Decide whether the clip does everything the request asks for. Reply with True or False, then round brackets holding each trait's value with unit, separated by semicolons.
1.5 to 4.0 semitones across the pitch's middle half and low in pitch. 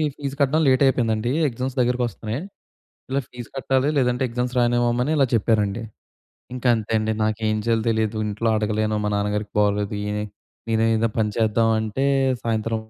True (2.5 semitones; 115 Hz)